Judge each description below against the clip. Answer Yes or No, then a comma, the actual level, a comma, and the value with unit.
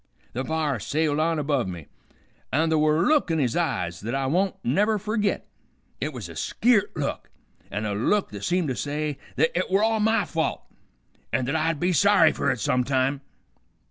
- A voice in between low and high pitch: Yes, medium, 155 Hz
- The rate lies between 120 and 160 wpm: No, average, 200 wpm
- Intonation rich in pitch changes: Yes, wide, 5.9 semitones